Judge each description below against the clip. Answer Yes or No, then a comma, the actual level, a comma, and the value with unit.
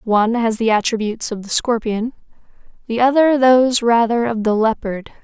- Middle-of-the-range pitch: No, high, 230 Hz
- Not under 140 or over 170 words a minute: Yes, average, 160 wpm